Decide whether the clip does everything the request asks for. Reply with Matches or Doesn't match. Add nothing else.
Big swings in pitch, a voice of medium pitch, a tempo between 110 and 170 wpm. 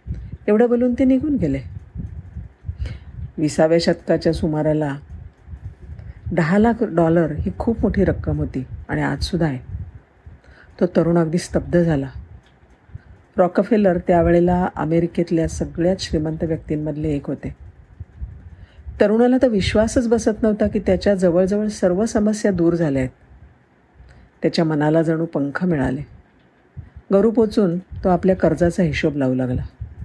Matches